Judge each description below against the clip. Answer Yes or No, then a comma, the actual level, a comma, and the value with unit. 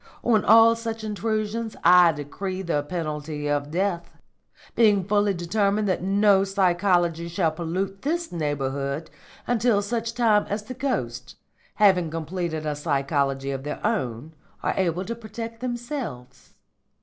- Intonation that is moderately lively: No, wide, 5.7 semitones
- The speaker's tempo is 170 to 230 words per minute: No, slow, 135 wpm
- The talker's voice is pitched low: No, medium, 185 Hz